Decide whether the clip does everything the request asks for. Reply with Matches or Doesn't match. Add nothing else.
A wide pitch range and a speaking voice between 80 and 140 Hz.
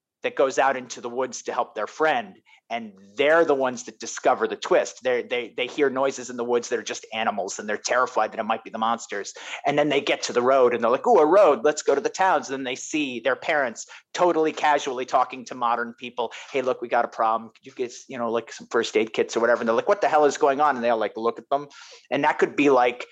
Matches